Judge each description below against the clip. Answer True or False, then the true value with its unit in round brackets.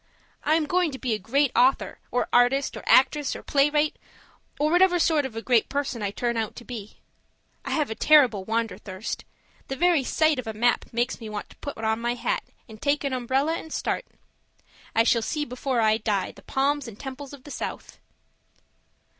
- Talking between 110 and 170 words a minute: False (200 wpm)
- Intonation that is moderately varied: True (4.4 semitones)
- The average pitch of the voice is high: True (260 Hz)